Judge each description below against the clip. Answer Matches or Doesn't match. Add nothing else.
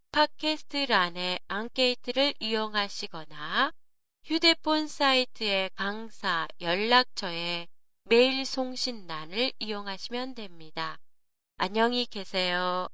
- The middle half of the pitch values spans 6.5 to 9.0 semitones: Doesn't match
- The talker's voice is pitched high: Matches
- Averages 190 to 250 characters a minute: Matches